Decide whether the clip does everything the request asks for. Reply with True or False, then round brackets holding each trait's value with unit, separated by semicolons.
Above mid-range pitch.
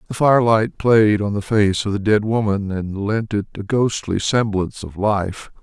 False (105 Hz)